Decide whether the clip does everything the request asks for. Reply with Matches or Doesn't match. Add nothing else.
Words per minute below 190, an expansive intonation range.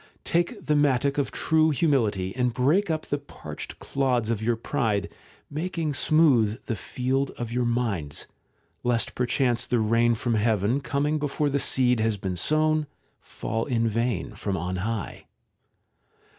Doesn't match